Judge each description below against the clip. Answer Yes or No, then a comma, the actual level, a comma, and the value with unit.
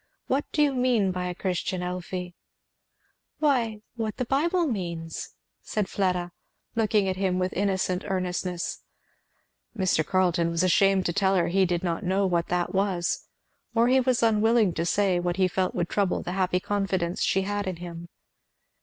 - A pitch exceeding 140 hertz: Yes, high, 190 Hz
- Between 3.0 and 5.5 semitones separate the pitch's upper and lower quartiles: No, narrow, 2.6 semitones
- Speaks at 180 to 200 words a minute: No, average, 170 wpm